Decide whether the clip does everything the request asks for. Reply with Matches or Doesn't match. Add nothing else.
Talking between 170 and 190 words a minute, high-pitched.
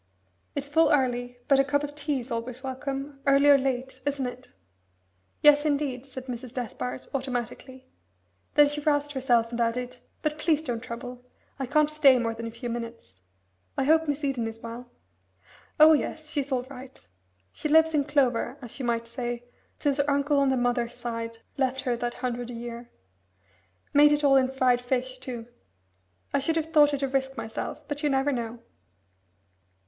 Matches